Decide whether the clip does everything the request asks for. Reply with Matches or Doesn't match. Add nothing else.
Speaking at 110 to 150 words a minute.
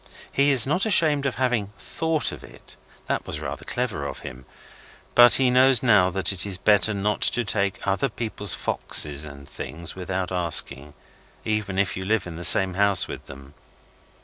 Doesn't match